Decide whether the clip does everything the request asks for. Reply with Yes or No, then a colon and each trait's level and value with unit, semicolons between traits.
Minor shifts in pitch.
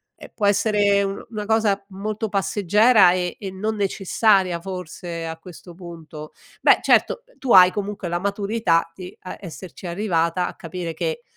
No: average, 3.1 semitones